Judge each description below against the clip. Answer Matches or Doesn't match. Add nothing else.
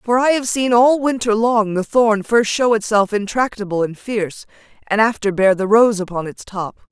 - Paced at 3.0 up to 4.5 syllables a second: Doesn't match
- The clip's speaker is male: Doesn't match